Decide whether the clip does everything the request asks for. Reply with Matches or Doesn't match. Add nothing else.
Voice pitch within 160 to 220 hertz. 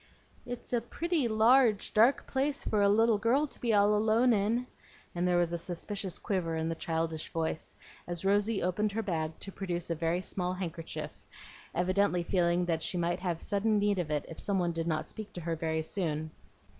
Matches